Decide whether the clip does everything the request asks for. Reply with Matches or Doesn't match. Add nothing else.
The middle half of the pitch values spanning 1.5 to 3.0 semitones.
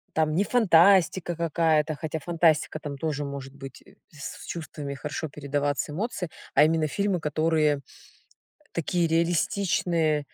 Matches